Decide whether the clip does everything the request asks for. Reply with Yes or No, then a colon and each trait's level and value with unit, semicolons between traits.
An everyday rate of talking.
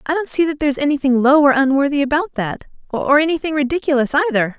Yes: average, 195 wpm